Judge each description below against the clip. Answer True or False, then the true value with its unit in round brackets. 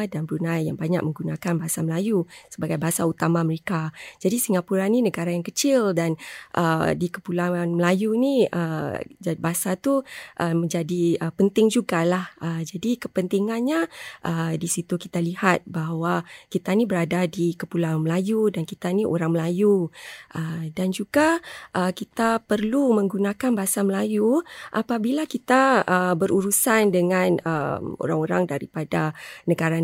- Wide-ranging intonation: False (4.0 semitones)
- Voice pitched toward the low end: False (180 Hz)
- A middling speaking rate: True (140 wpm)